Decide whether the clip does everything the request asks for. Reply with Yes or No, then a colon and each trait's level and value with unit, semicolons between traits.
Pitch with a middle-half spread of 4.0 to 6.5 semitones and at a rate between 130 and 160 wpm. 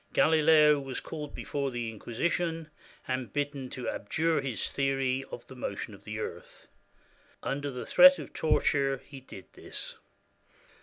No: average, 3.0 semitones; average, 150 wpm